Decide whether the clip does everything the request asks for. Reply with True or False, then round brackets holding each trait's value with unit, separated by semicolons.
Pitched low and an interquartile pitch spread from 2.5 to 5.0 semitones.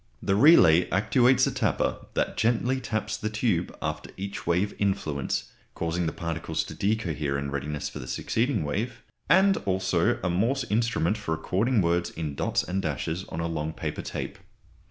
False (90 Hz; 5.4 semitones)